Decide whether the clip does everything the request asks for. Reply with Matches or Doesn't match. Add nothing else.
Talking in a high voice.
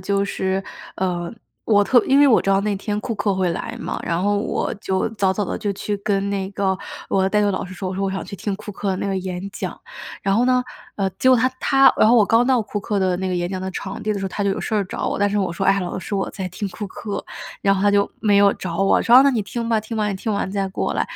Matches